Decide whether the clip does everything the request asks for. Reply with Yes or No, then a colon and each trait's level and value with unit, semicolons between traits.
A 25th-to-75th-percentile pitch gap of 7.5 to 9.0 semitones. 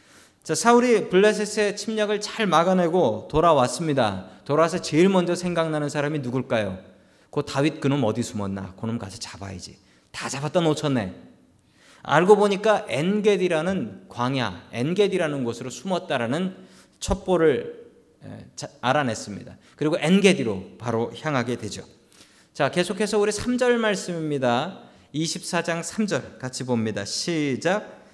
Yes: wide, 8.1 semitones